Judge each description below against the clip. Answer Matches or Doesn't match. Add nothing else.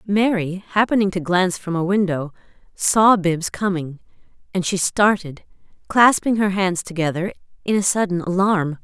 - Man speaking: Doesn't match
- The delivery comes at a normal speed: Matches